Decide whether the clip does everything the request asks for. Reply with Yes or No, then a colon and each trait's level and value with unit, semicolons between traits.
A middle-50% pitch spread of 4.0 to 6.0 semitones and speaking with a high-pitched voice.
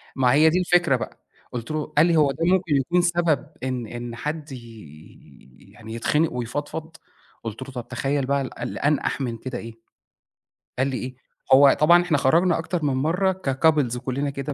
No: average, 4.4 semitones; medium, 140 Hz